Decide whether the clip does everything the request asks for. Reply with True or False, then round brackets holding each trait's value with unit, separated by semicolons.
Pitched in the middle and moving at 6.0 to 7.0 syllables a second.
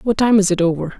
False (195 Hz; 6.3 syllables/s)